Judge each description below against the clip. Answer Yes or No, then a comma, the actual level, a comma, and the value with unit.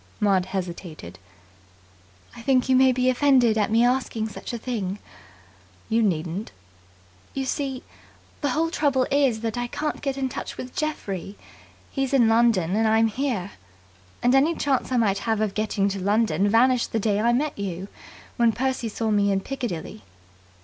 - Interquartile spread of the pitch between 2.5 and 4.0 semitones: No, average, 4.4 semitones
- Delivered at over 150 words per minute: Yes, average, 170 wpm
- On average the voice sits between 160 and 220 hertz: No, high, 230 Hz